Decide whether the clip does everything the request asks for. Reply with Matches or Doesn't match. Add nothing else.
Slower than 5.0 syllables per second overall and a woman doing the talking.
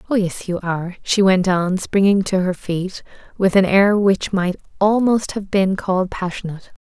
Matches